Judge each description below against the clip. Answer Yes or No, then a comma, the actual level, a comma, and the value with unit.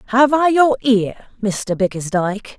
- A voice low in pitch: No, high, 225 Hz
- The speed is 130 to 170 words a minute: Yes, average, 140 wpm